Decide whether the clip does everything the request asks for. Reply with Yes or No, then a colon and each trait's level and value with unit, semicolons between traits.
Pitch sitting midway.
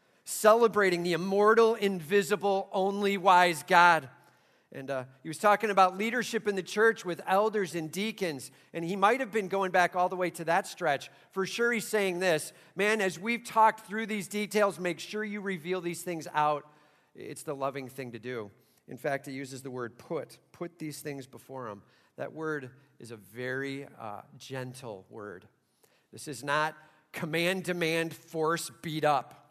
Yes: medium, 170 Hz